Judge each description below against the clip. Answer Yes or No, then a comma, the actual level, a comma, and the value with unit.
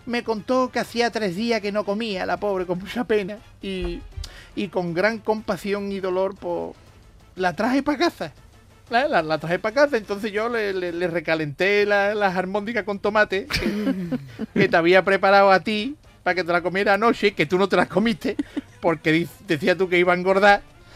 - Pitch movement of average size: Yes, average, 3.3 semitones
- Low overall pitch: No, high, 200 Hz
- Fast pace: Yes, fast, 205 wpm